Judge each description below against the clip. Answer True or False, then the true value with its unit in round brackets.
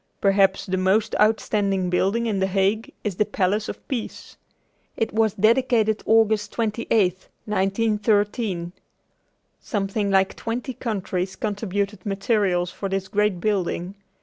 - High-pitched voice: True (205 Hz)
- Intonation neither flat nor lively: False (2.3 semitones)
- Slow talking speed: True (120 wpm)